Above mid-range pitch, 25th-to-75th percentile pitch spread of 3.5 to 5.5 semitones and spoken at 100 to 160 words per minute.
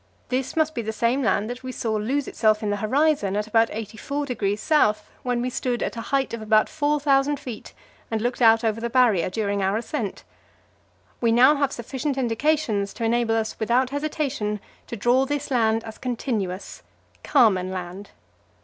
No: high, 235 Hz; average, 3.8 semitones; average, 175 wpm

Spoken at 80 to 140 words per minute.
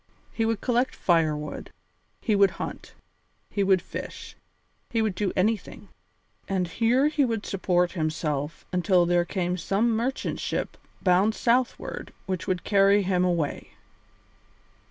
Yes: slow, 135 wpm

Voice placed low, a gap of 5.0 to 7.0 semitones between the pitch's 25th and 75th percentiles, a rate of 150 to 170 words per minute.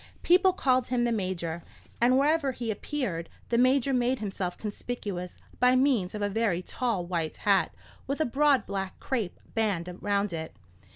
No: high, 225 Hz; wide, 5.6 semitones; average, 165 wpm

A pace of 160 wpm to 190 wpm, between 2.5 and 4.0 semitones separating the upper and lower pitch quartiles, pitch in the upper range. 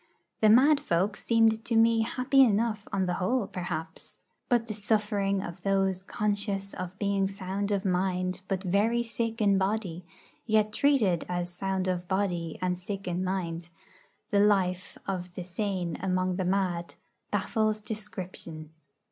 No: average, 150 wpm; average, 2.8 semitones; high, 195 Hz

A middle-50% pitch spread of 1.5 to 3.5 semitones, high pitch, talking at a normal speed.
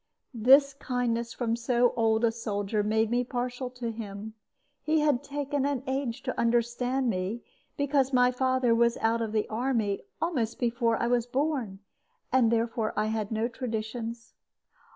Yes: narrow, 2.4 semitones; high, 235 Hz; average, 155 wpm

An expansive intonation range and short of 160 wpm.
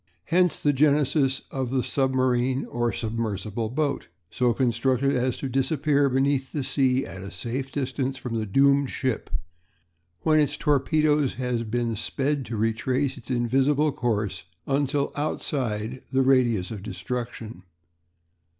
No: average, 3.1 semitones; average, 140 wpm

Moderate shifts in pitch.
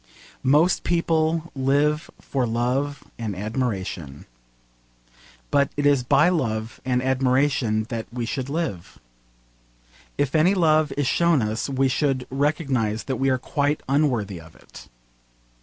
Yes: average, 4.0 semitones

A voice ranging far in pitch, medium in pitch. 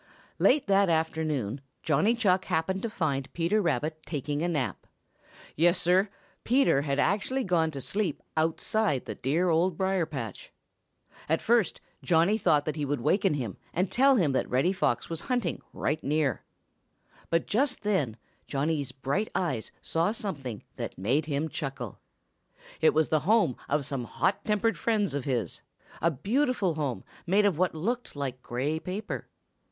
Yes: wide, 5.7 semitones; medium, 160 Hz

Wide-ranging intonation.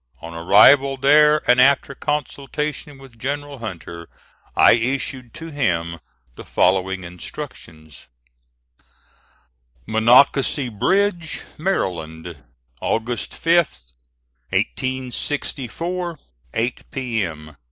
Yes: wide, 7.5 semitones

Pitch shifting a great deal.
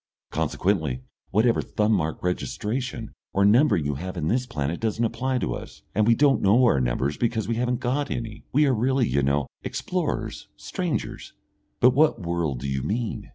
Yes: wide, 7.3 semitones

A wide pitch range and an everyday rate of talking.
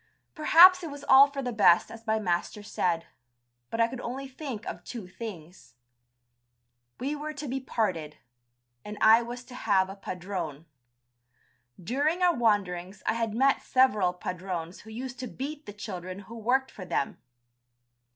Yes: wide, 6.1 semitones; average, 160 wpm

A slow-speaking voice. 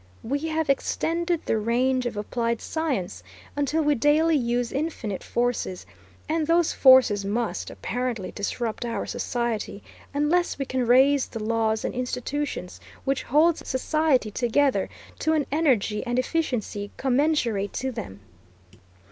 Yes: slow, 130 wpm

